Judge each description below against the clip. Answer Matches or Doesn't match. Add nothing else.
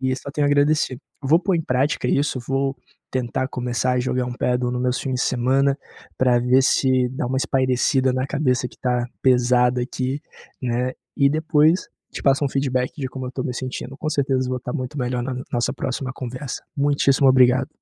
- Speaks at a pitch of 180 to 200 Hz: Doesn't match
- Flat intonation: Matches